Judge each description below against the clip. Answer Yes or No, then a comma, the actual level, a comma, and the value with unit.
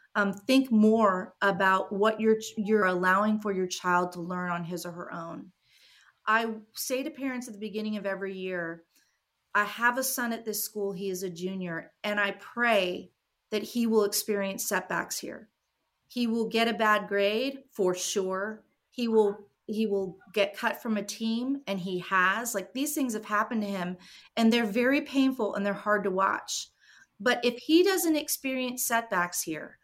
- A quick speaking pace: No, average, 185 wpm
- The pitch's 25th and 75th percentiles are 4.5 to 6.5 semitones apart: No, average, 3.6 semitones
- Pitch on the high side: Yes, high, 210 Hz